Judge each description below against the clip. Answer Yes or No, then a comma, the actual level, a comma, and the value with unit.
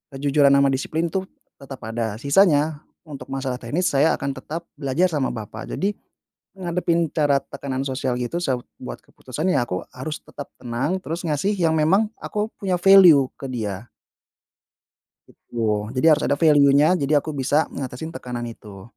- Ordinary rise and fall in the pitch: Yes, average, 4.3 semitones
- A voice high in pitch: No, medium, 140 Hz